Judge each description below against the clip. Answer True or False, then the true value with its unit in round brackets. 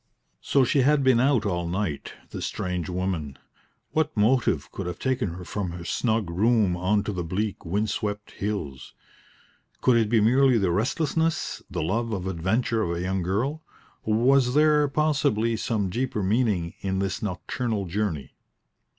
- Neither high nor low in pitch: False (105 Hz)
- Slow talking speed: False (165 wpm)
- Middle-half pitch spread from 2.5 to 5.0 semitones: False (5.4 semitones)